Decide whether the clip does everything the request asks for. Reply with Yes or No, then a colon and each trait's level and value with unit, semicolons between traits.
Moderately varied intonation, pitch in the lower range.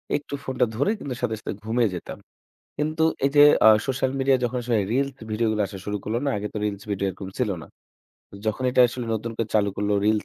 Yes: average, 3.9 semitones; low, 115 Hz